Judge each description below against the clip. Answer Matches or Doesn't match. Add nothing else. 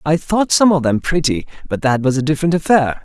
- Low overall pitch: Doesn't match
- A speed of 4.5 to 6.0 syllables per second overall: Matches